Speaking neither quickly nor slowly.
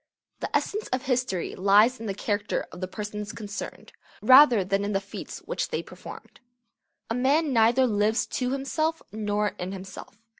Yes: average, 165 wpm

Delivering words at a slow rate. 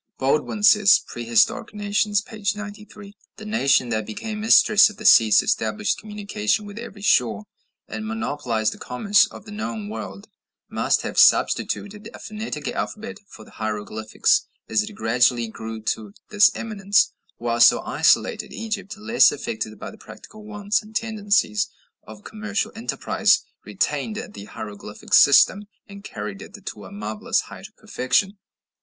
No: average, 145 wpm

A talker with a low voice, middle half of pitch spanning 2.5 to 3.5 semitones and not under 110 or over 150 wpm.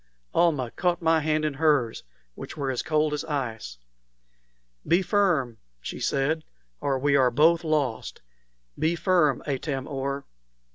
No: medium, 150 Hz; average, 3.2 semitones; average, 140 wpm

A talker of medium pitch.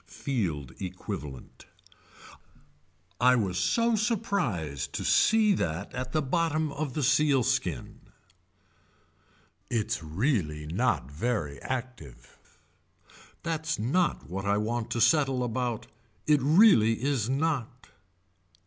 No: low, 120 Hz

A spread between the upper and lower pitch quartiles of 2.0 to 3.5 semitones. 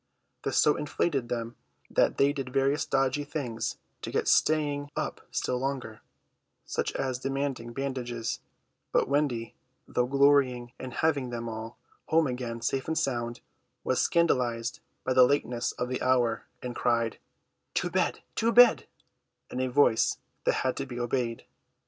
Yes: average, 2.9 semitones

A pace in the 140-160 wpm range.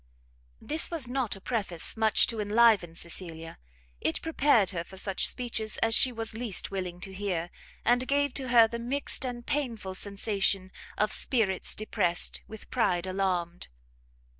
Yes: average, 155 wpm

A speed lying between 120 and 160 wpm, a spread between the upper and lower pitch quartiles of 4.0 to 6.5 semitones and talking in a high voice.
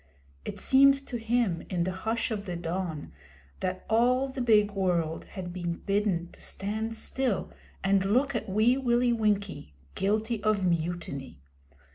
Yes: average, 150 wpm; average, 4.6 semitones; high, 205 Hz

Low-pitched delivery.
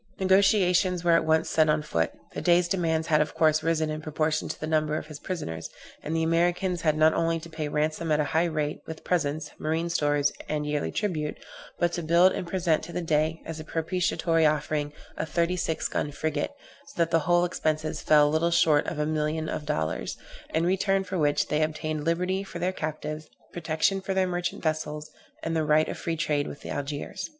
No: medium, 160 Hz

